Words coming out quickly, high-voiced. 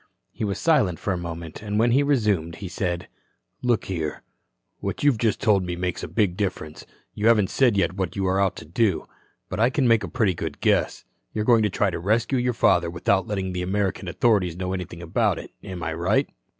No: fast, 220 wpm; very low, 95 Hz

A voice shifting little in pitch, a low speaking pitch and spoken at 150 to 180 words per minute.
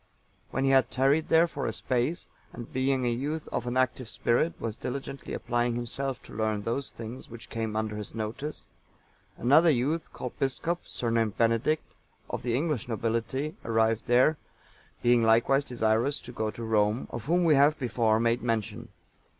No: average, 3.3 semitones; low, 120 Hz; average, 170 wpm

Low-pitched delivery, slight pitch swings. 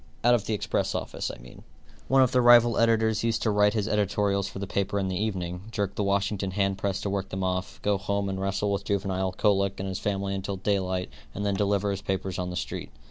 Yes: low, 100 Hz; narrow, 1.4 semitones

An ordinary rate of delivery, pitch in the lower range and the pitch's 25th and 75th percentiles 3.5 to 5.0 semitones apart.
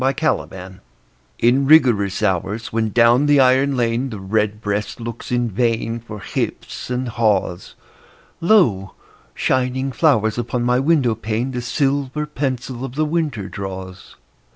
No: slow, 130 wpm; low, 120 Hz; average, 3.9 semitones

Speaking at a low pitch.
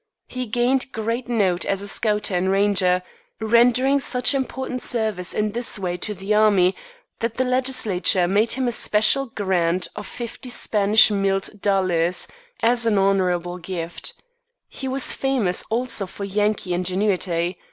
No: high, 210 Hz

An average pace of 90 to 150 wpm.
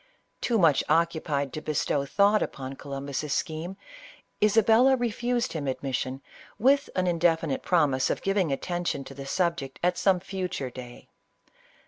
Yes: average, 140 wpm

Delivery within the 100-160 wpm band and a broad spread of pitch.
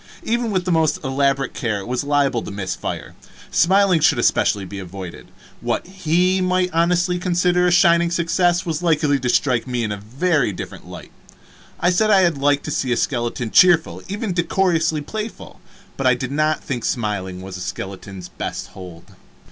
No: average, 180 wpm; wide, 6.9 semitones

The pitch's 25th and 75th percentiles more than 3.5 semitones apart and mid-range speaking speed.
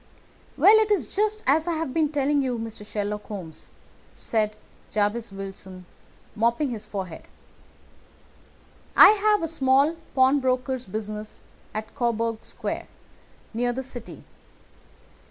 No: wide, 5.5 semitones; slow, 120 wpm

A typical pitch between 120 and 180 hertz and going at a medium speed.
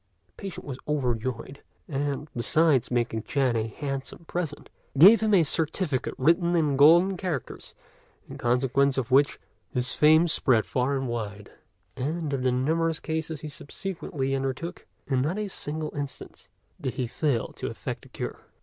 Yes: medium, 140 Hz; average, 160 wpm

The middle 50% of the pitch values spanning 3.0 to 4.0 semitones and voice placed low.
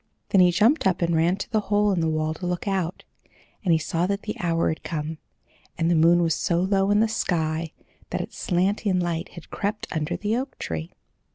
No: average, 3.6 semitones; medium, 175 Hz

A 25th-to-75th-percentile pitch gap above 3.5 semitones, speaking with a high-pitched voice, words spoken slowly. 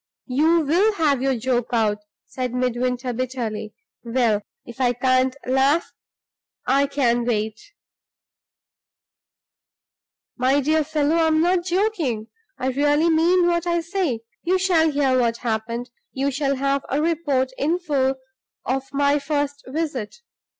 Yes: average, 4.3 semitones; very high, 275 Hz; slow, 130 wpm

